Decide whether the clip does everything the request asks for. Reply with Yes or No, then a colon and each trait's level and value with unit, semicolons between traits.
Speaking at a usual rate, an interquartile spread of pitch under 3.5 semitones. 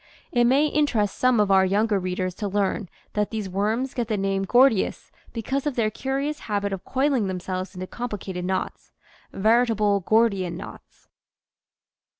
No: average, 155 wpm; average, 4.0 semitones